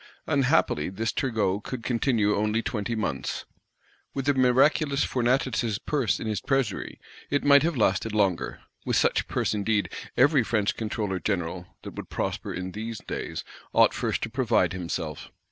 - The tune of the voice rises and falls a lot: No, average, 4.5 semitones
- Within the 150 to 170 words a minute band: Yes, average, 155 wpm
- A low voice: Yes, low, 110 Hz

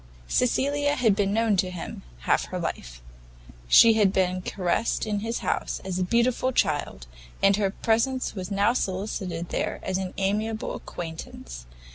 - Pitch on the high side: Yes, high, 200 Hz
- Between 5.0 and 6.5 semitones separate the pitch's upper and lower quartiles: No, average, 3.8 semitones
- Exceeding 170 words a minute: No, average, 155 wpm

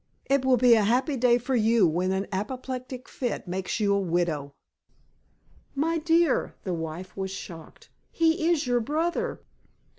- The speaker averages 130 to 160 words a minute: Yes, average, 155 wpm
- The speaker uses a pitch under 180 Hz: No, high, 235 Hz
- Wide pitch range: Yes, wide, 6.2 semitones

